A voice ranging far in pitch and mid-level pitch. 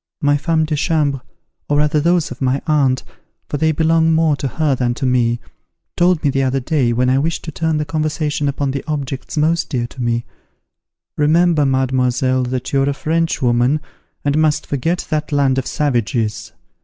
No: average, 3.3 semitones; medium, 145 Hz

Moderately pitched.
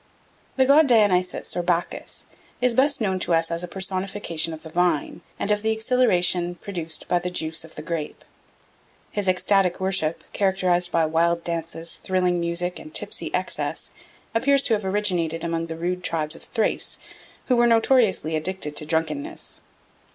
Yes: medium, 180 Hz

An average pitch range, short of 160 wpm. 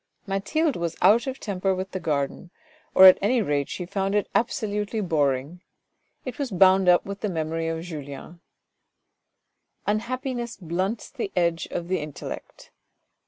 Yes: average, 4.2 semitones; average, 150 wpm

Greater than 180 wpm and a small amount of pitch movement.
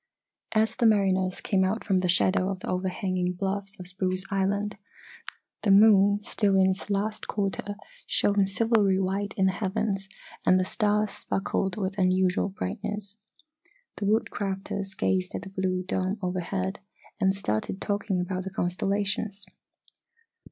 No: average, 145 wpm; narrow, 1.5 semitones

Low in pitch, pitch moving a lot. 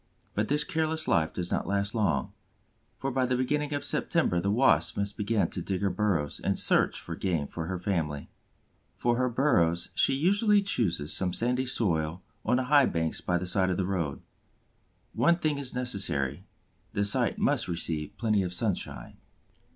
Yes: low, 100 Hz; wide, 6.7 semitones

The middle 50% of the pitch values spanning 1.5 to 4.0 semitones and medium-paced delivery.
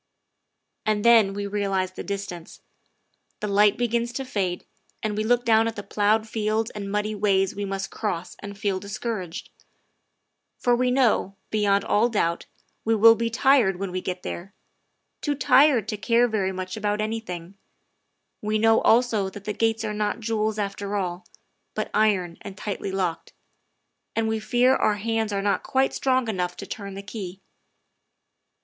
Yes: narrow, 2.4 semitones; average, 170 wpm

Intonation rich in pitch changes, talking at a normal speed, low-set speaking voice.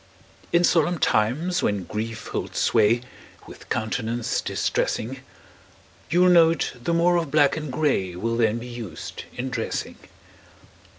No: wide, 6.6 semitones; slow, 130 wpm; low, 125 Hz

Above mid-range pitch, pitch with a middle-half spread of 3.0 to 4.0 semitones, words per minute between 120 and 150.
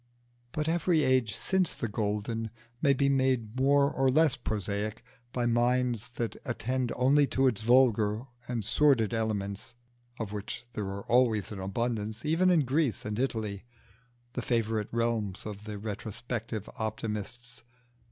No: low, 115 Hz; average, 3.5 semitones; average, 140 wpm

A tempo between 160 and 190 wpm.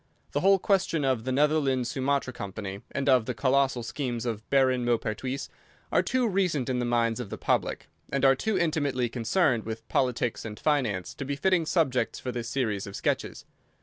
Yes: average, 185 wpm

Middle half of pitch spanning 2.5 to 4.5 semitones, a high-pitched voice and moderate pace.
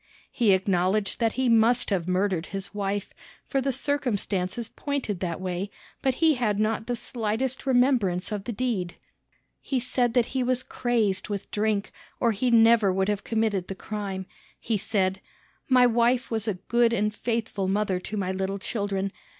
Yes: average, 3.8 semitones; high, 215 Hz; average, 165 wpm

